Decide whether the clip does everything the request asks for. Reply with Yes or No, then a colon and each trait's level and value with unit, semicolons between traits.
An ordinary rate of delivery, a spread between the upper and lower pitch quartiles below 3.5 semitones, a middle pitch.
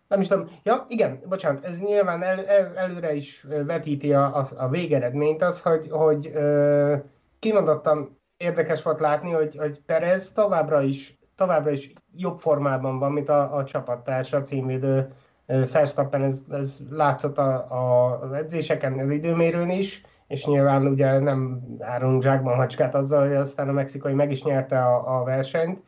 No: fast, 160 wpm; average, 3.0 semitones; medium, 145 Hz